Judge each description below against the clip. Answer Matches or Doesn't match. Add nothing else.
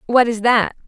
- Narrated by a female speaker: Matches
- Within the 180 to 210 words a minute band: Matches